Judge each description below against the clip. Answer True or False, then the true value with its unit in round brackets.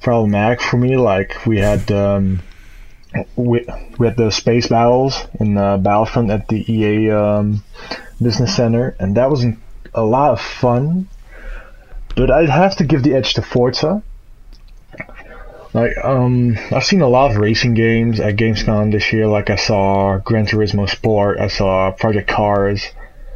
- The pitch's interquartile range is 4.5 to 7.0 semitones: False (3.2 semitones)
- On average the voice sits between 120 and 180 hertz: False (110 Hz)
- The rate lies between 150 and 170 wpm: True (160 wpm)